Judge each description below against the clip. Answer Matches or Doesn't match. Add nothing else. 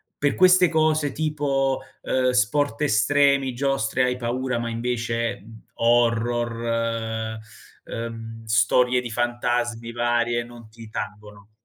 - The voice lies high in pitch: Doesn't match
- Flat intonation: Matches